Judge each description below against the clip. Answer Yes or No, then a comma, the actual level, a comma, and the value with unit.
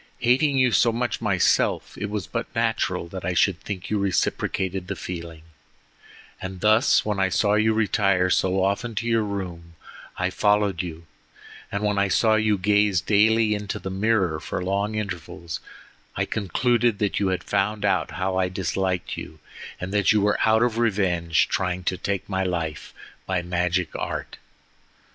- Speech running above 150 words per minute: Yes, average, 170 wpm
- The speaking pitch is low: Yes, low, 100 Hz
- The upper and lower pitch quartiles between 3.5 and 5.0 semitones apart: No, average, 2.8 semitones